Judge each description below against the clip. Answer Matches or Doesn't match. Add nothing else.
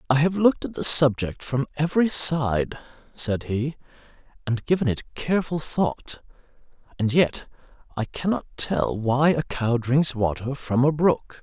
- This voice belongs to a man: Matches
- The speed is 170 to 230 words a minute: Doesn't match